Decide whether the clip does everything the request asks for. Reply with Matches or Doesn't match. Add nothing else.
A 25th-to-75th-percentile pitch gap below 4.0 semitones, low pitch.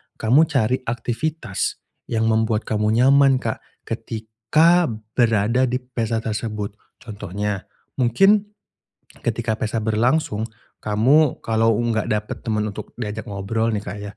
Matches